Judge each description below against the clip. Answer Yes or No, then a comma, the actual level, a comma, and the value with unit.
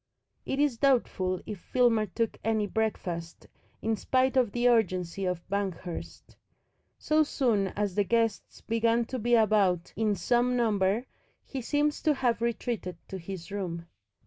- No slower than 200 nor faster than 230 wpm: No, average, 145 wpm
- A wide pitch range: No, average, 4.2 semitones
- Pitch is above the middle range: Yes, high, 220 Hz